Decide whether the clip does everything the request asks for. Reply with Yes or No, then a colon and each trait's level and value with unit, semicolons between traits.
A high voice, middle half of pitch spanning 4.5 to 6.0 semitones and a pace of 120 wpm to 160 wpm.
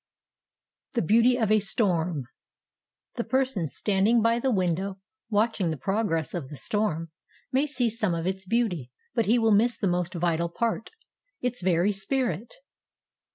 Yes: high, 205 Hz; average, 5.0 semitones; average, 150 wpm